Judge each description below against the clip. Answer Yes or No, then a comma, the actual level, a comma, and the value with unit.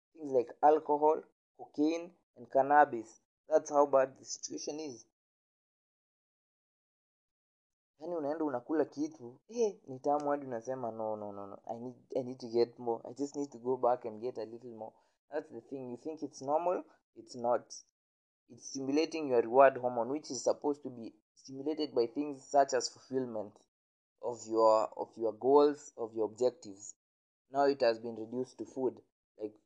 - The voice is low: Yes, low, 130 Hz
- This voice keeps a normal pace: Yes, average, 160 wpm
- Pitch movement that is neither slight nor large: Yes, average, 4.1 semitones